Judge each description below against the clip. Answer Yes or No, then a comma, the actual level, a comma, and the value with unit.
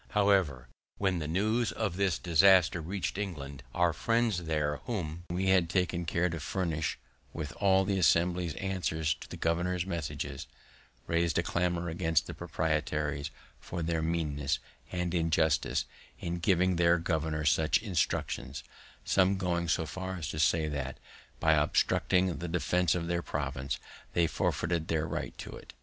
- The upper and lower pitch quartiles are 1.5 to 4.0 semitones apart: Yes, narrow, 2.6 semitones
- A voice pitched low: Yes, very low, 85 Hz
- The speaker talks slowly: No, average, 155 wpm